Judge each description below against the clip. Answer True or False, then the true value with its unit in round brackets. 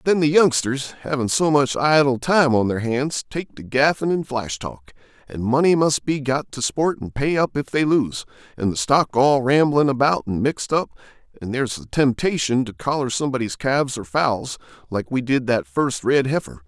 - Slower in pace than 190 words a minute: False (200 wpm)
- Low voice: True (130 Hz)